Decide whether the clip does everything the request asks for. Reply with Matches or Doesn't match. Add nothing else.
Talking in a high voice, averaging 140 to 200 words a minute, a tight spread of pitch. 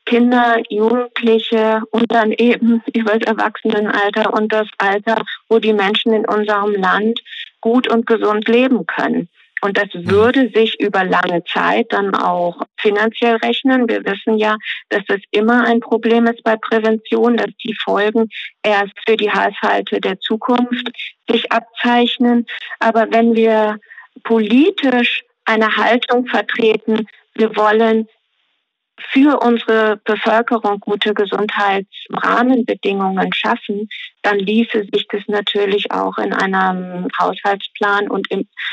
Doesn't match